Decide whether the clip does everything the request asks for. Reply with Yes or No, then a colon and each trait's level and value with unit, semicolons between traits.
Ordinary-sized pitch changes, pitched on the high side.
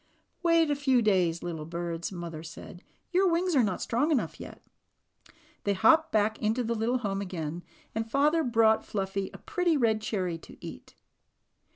No: wide, 7.6 semitones; high, 220 Hz